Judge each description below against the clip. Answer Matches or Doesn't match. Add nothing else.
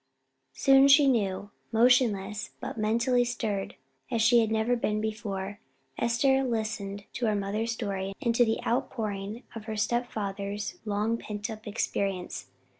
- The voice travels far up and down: Doesn't match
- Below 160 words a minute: Matches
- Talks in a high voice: Matches